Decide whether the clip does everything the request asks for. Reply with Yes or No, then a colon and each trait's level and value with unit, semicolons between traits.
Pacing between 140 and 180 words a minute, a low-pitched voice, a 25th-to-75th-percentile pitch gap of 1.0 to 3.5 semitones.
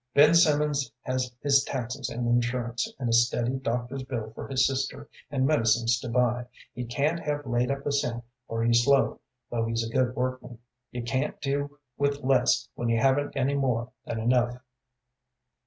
Yes: average, 175 wpm; low, 125 Hz; average, 2.7 semitones